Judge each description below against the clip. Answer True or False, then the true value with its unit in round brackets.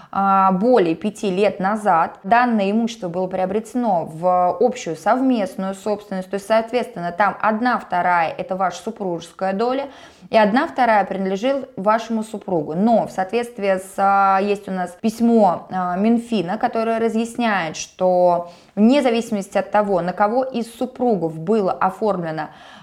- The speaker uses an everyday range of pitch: True (3.4 semitones)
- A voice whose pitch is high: True (205 Hz)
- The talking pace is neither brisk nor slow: True (130 wpm)